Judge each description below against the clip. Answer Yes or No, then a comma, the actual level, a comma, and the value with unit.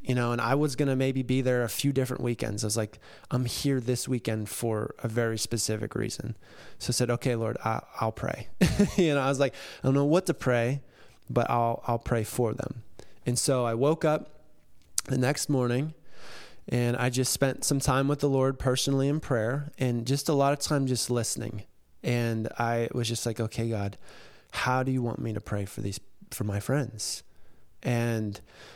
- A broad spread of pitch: No, average, 2.9 semitones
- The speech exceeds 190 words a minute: Yes, fast, 205 wpm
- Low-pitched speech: Yes, low, 125 Hz